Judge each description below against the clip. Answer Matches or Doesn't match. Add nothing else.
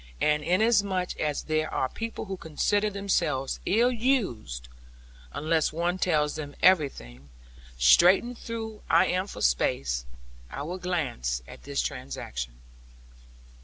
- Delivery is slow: Matches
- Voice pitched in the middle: Matches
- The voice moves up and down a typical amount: Doesn't match